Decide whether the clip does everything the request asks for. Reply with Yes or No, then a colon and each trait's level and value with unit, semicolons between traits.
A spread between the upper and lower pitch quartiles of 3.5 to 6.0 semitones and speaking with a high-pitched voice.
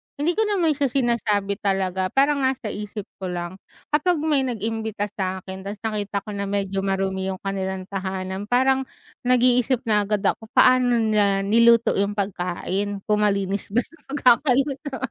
Yes: average, 4.5 semitones; high, 210 Hz